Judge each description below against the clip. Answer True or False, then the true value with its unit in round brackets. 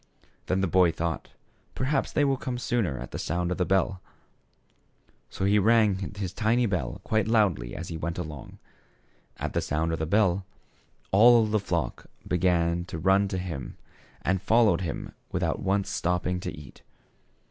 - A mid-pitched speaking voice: False (95 Hz)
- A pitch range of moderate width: True (3.9 semitones)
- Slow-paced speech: False (185 wpm)